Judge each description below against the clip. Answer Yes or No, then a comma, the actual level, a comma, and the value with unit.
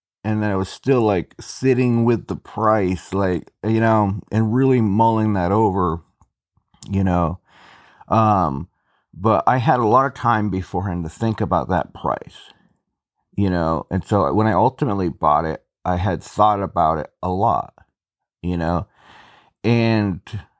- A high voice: No, low, 100 Hz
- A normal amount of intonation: Yes, average, 3.7 semitones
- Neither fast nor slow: Yes, average, 155 wpm